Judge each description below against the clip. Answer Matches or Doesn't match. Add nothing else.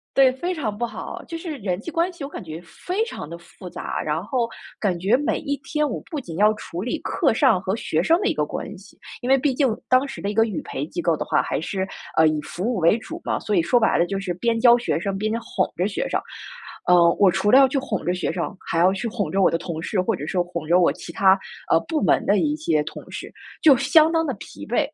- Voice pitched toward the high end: Matches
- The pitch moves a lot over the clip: Matches